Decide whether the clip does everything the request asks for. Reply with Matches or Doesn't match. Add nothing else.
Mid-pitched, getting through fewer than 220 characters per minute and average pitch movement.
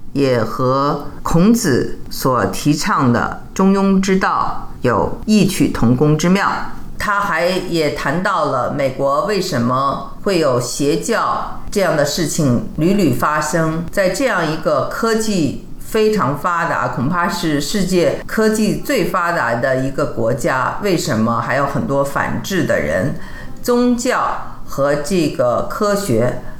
Doesn't match